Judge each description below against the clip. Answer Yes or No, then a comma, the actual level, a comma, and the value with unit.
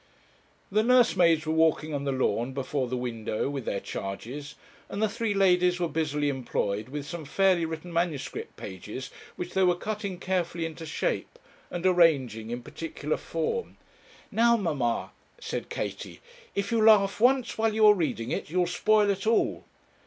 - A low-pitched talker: No, medium, 165 Hz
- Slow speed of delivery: No, average, 165 wpm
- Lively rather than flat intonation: Yes, wide, 6.1 semitones